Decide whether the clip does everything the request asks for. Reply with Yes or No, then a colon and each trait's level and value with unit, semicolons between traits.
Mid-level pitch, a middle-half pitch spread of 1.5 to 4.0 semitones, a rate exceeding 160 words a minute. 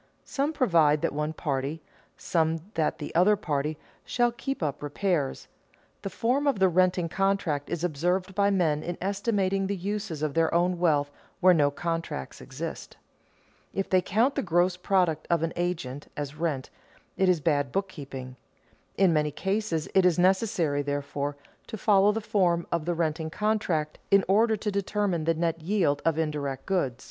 No: medium, 170 Hz; average, 4.4 semitones; average, 170 wpm